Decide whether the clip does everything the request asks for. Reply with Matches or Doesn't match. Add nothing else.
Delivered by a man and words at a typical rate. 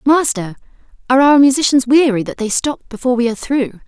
Doesn't match